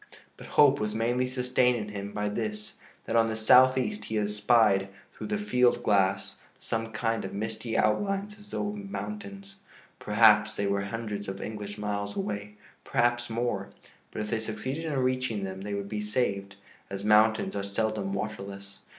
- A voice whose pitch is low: Yes, low, 110 Hz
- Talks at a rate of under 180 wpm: Yes, average, 170 wpm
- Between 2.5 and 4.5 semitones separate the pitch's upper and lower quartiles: Yes, average, 3.5 semitones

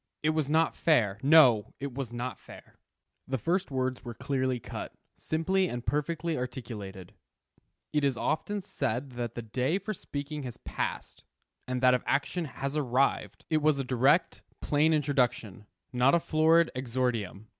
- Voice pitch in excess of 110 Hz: Yes, low, 135 Hz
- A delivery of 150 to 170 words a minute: Yes, average, 155 wpm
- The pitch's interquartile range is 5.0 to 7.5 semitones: No, average, 4.1 semitones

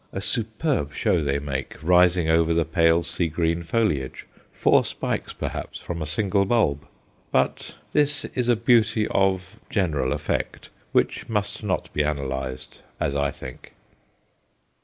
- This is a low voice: Yes, very low, 85 Hz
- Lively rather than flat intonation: Yes, wide, 5.9 semitones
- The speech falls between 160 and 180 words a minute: No, average, 140 wpm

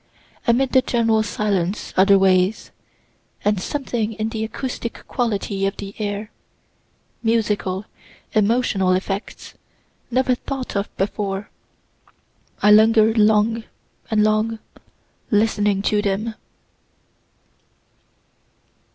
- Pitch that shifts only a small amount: Yes, narrow, 2.2 semitones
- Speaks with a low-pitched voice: No, high, 215 Hz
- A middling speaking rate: No, slow, 90 wpm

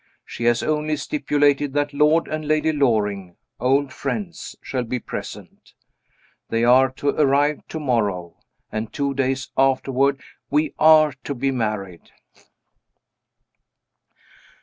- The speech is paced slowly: Yes, slow, 115 wpm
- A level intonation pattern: No, average, 3.9 semitones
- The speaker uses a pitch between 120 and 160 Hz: Yes, low, 135 Hz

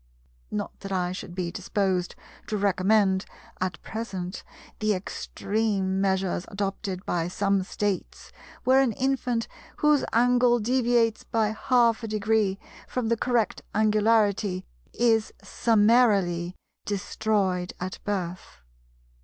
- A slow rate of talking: Yes, slow, 110 wpm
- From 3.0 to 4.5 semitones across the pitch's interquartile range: Yes, average, 3.3 semitones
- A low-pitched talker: No, high, 205 Hz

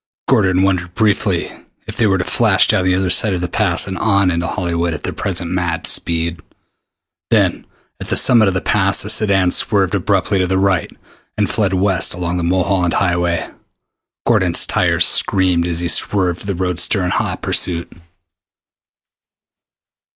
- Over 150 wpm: Yes, average, 165 wpm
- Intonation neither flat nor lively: No, narrow, 2.0 semitones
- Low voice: Yes, very low, 90 Hz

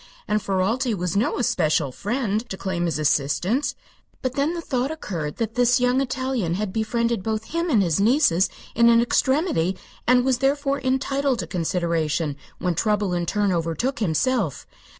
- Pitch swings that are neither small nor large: No, wide, 6.3 semitones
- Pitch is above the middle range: Yes, high, 220 Hz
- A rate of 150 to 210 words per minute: Yes, average, 165 wpm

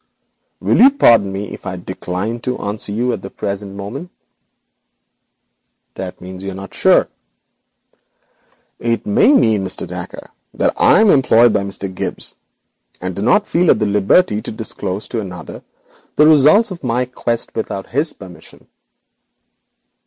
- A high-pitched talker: No, low, 110 Hz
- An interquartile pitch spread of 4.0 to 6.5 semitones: Yes, average, 4.6 semitones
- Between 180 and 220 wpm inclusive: No, average, 145 wpm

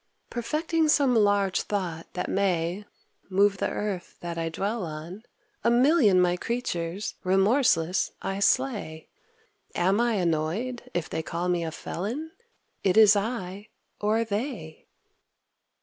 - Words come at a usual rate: No, slow, 130 wpm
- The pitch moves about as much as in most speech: Yes, average, 4.9 semitones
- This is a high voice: Yes, high, 200 Hz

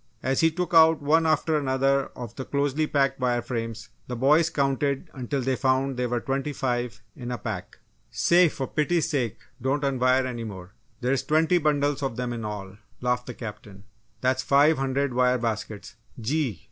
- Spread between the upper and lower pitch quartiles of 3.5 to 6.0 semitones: No, average, 3.0 semitones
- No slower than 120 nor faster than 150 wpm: No, average, 180 wpm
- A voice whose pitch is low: Yes, low, 130 Hz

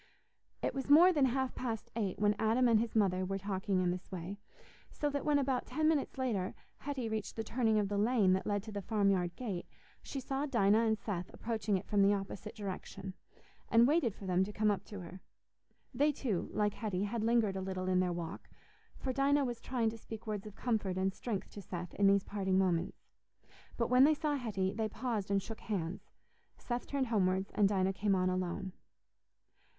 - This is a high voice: Yes, high, 210 Hz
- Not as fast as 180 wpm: No, fast, 205 wpm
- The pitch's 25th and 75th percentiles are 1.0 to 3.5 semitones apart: No, average, 4.0 semitones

